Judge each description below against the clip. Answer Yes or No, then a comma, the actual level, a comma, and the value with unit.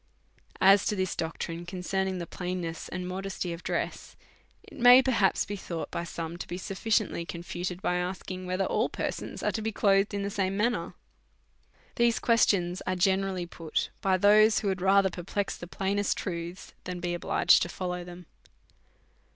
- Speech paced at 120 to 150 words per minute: No, average, 175 wpm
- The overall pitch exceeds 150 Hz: Yes, medium, 185 Hz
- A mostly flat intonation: Yes, narrow, 2.1 semitones